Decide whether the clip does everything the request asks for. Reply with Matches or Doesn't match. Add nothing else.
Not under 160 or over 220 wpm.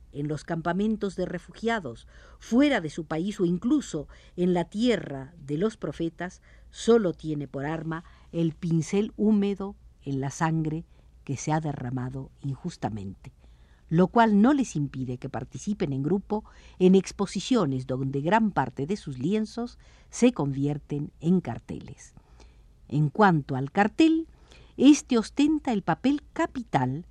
Doesn't match